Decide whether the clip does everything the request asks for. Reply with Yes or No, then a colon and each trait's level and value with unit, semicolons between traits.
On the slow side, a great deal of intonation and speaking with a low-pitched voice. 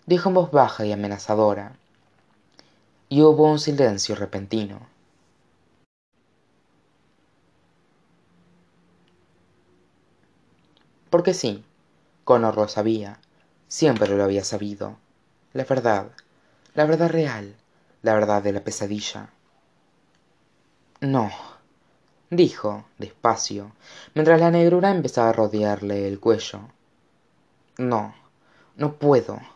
Yes: slow, 90 wpm; wide, 6.3 semitones; low, 110 Hz